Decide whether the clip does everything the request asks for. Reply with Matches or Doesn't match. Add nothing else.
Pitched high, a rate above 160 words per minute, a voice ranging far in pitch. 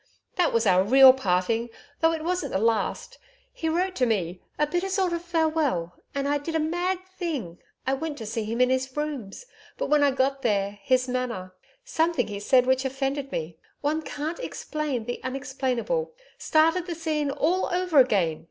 Matches